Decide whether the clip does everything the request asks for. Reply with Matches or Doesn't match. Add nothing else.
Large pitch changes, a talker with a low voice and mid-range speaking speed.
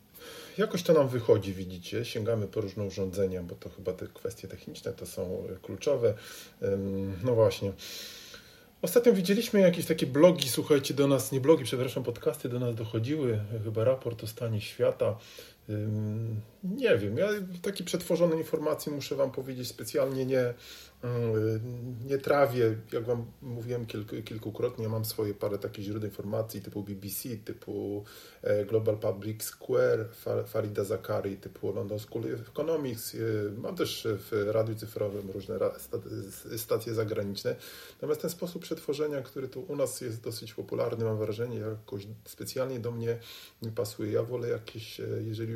Matches